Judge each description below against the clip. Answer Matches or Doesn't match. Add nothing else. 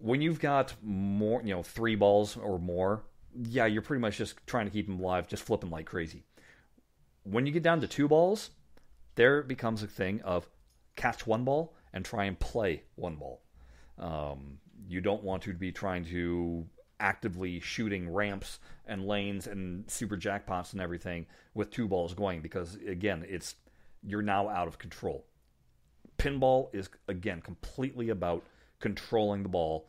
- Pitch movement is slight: Doesn't match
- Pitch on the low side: Matches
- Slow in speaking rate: Doesn't match